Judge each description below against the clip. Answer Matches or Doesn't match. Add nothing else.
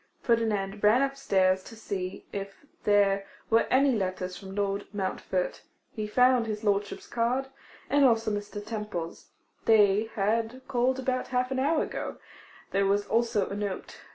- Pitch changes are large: Doesn't match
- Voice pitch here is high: Matches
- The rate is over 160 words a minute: Doesn't match